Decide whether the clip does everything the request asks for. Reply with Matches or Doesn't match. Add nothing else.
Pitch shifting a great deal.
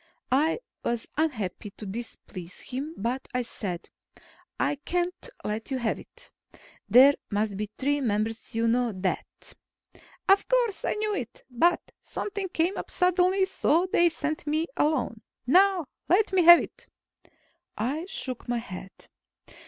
Matches